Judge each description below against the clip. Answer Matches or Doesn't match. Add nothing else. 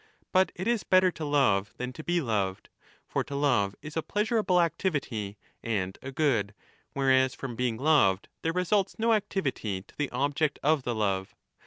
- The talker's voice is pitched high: Doesn't match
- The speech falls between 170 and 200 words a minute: Matches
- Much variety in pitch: Matches